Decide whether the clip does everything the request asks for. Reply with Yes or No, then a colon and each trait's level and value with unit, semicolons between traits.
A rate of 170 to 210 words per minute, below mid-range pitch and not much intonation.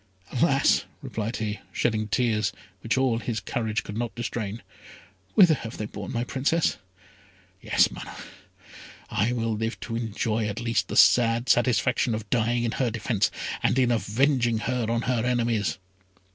No: average, 155 wpm; low, 115 Hz; narrow, 1.9 semitones